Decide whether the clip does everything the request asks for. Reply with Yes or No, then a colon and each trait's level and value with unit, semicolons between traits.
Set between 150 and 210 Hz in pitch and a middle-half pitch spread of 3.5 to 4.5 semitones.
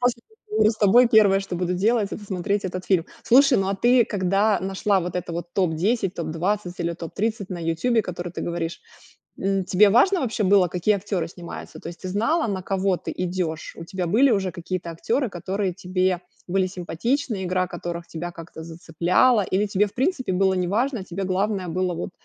No: high, 190 Hz; average, 3.1 semitones